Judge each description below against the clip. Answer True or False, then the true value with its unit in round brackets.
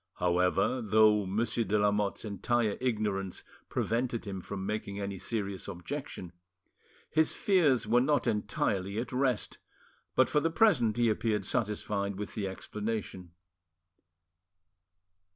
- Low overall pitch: True (105 Hz)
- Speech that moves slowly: True (120 wpm)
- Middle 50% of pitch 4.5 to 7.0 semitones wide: False (3.3 semitones)